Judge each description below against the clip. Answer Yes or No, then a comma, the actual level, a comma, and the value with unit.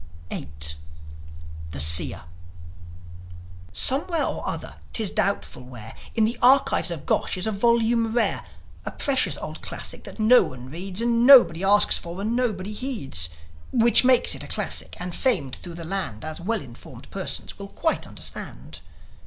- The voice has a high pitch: Yes, high, 200 Hz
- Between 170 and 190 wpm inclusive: No, average, 155 wpm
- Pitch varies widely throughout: Yes, wide, 6.8 semitones